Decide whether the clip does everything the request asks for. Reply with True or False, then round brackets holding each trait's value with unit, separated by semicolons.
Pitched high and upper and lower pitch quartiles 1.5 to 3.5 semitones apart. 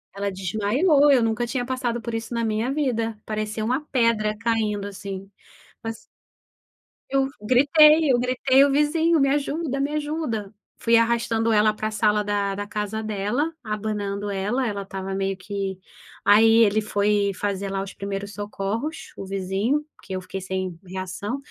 False (215 Hz; 3.9 semitones)